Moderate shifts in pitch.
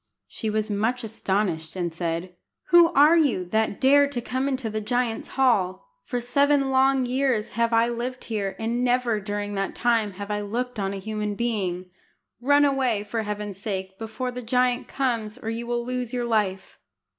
Yes: average, 3.5 semitones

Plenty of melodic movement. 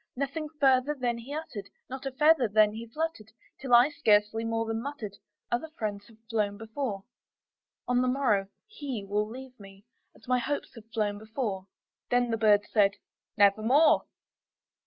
No: average, 4.1 semitones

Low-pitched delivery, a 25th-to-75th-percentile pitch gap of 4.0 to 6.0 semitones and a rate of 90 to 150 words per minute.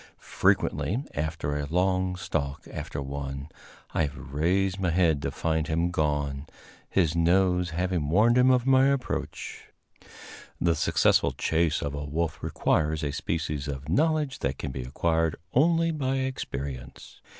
Yes: very low, 80 Hz; average, 4.7 semitones; average, 145 wpm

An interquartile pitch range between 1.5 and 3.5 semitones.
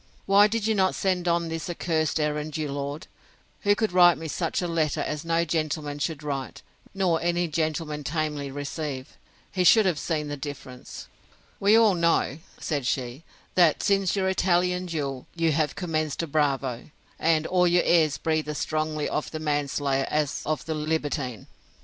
Yes: average, 3.0 semitones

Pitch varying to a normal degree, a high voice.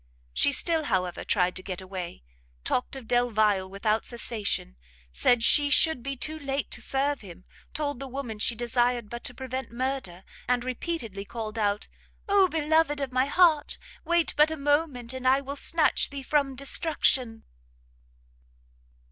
Yes: average, 4.8 semitones; very high, 255 Hz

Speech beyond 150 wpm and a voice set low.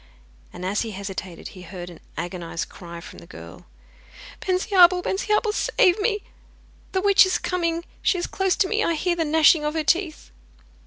No: average, 175 wpm; very high, 330 Hz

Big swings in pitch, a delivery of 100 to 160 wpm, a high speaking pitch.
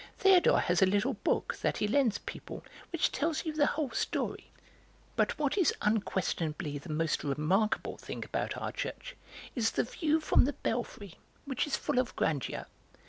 No: wide, 8.1 semitones; average, 170 wpm; high, 230 Hz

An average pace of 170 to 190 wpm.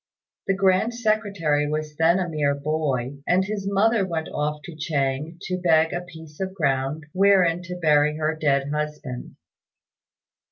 No: average, 155 wpm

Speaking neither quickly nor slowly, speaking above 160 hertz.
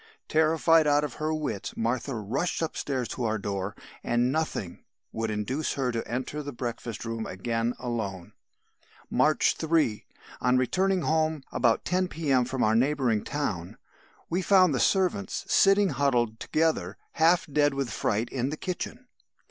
No: average, 150 wpm; low, 135 Hz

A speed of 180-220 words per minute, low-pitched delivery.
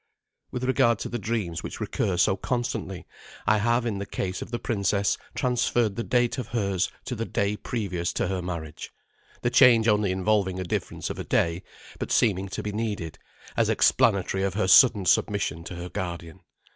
Yes: average, 185 wpm; low, 100 Hz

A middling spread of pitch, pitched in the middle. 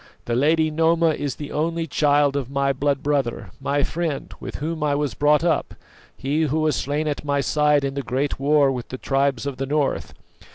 No: narrow, 1.8 semitones; medium, 145 Hz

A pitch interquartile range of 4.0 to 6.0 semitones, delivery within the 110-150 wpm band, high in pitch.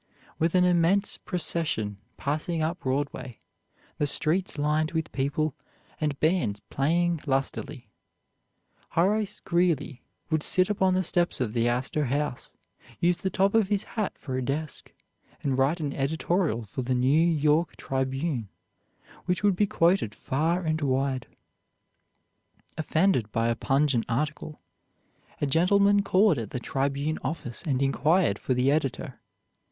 No: average, 4.6 semitones; average, 140 wpm; medium, 155 Hz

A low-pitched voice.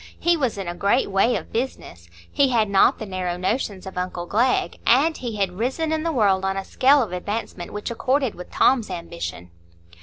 No: high, 210 Hz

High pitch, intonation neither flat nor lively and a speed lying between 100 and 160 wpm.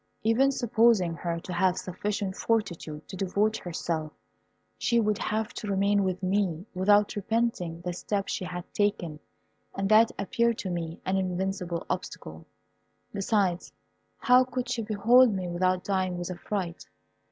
Yes: high, 195 Hz; average, 3.3 semitones; average, 145 wpm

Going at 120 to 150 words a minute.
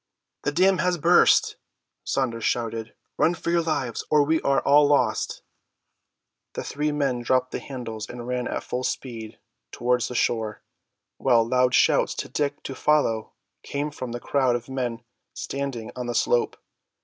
No: average, 160 wpm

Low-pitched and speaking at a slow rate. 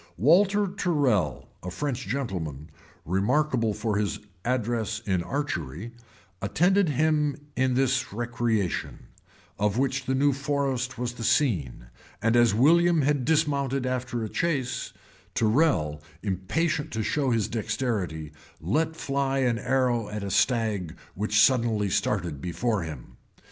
Yes: low, 120 Hz; slow, 130 wpm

